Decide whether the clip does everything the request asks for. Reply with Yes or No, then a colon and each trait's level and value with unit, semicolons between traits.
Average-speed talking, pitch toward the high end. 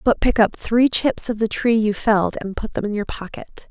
No: fast, 260 wpm; high, 220 Hz